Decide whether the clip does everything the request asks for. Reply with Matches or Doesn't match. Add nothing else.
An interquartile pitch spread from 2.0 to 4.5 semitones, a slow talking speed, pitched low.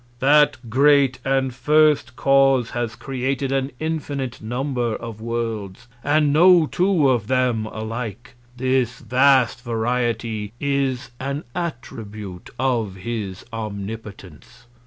Matches